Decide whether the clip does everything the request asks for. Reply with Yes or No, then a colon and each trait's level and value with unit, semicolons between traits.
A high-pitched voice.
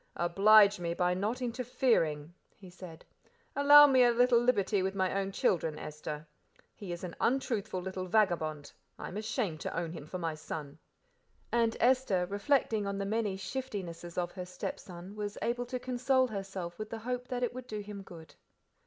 Yes: high, 200 Hz